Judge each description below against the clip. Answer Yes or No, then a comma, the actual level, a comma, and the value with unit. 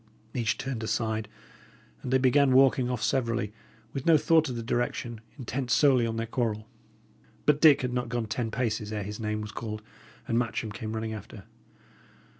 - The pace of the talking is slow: No, average, 180 wpm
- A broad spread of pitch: No, average, 2.8 semitones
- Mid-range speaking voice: No, low, 120 Hz